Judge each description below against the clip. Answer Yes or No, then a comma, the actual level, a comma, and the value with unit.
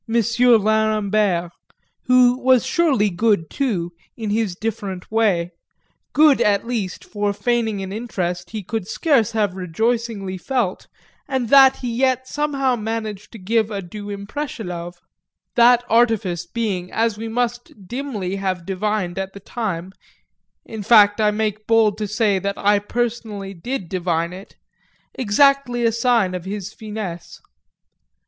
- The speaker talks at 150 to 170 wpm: No, average, 140 wpm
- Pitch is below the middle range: No, high, 215 Hz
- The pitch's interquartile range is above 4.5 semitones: No, average, 3.5 semitones